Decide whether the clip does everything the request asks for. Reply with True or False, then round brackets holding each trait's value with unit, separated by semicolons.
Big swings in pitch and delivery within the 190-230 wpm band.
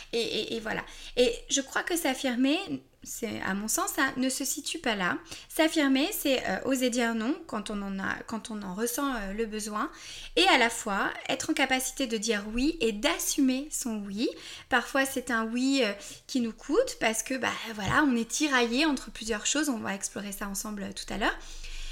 False (4.5 semitones; 215 wpm)